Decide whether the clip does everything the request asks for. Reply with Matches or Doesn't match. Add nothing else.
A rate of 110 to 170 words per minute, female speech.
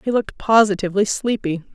Matches